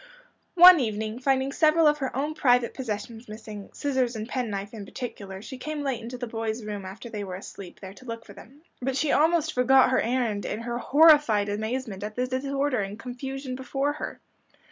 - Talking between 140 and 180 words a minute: No, average, 200 wpm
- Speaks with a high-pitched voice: Yes, high, 245 Hz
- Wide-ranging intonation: No, average, 4.0 semitones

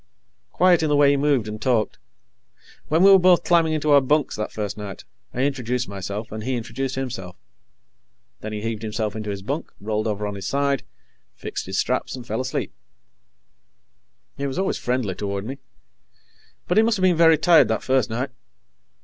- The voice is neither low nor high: No, low, 125 Hz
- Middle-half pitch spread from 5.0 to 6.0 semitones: Yes, wide, 5.6 semitones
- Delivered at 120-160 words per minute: No, average, 190 wpm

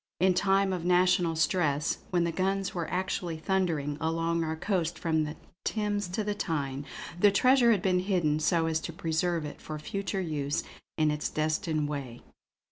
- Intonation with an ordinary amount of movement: Yes, average, 3.4 semitones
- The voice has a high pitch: No, medium, 170 Hz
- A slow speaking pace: No, average, 175 wpm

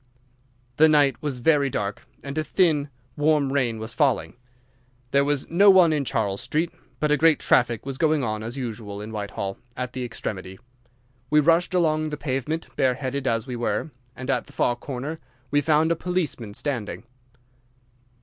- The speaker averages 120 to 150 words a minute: No, average, 175 wpm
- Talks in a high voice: No, medium, 140 Hz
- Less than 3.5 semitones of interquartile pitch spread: No, average, 4.5 semitones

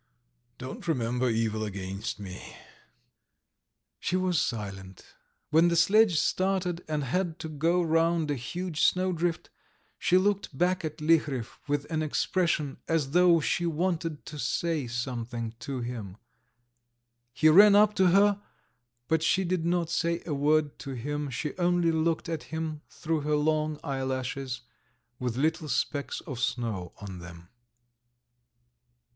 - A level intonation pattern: No, average, 5.2 semitones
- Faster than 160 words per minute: No, average, 140 wpm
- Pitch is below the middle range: No, medium, 155 Hz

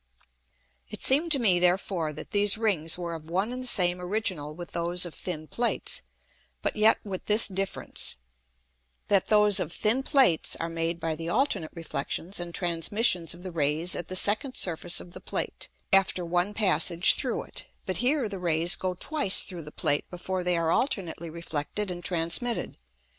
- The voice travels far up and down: No, average, 3.7 semitones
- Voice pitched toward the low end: No, medium, 180 Hz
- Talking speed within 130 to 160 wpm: No, average, 180 wpm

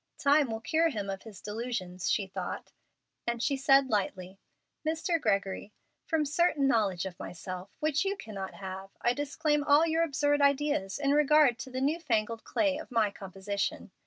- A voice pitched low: No, very high, 255 Hz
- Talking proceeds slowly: No, average, 170 wpm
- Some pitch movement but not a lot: No, wide, 6.9 semitones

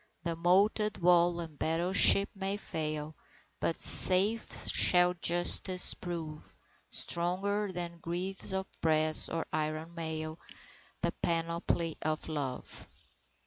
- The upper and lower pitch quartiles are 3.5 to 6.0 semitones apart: No, narrow, 2.5 semitones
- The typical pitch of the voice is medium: Yes, medium, 170 Hz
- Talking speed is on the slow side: Yes, slow, 105 wpm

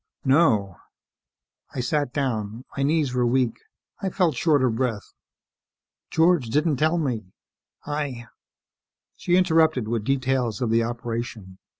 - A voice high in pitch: No, low, 130 Hz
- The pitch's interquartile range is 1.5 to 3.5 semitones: No, average, 4.7 semitones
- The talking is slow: Yes, slow, 130 wpm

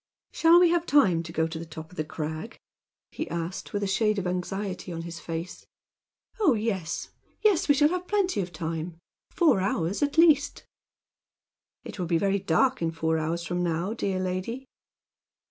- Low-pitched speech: No, medium, 185 Hz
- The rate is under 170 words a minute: No, average, 180 wpm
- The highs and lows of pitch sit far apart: Yes, wide, 7.6 semitones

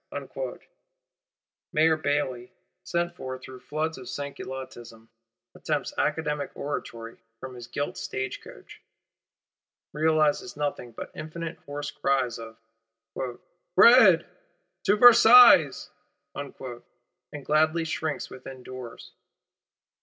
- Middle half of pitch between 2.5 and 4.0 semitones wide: Yes, average, 3.7 semitones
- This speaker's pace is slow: Yes, slow, 90 wpm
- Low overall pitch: No, medium, 145 Hz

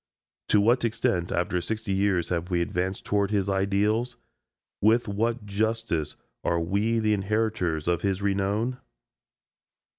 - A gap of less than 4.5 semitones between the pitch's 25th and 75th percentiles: Yes, average, 3.3 semitones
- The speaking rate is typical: No, slow, 130 wpm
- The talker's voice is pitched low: Yes, low, 100 Hz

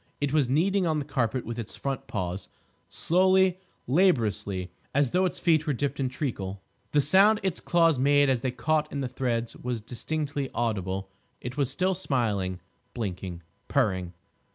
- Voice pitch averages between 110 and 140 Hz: Yes, low, 135 Hz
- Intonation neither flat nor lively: No, wide, 6.0 semitones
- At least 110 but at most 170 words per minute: Yes, average, 160 wpm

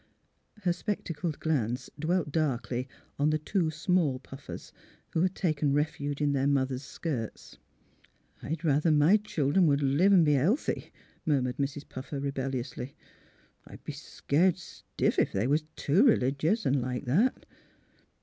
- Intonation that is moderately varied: Yes, average, 3.4 semitones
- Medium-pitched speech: Yes, medium, 145 Hz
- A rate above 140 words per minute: Yes, average, 150 wpm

